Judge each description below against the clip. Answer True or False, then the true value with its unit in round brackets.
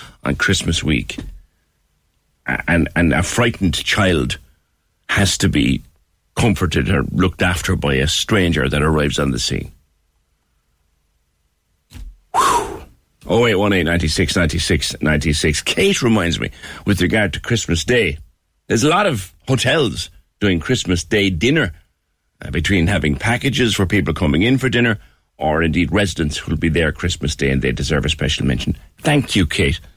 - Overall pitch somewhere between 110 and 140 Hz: False (85 Hz)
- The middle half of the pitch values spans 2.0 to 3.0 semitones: False (4.7 semitones)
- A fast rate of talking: False (140 wpm)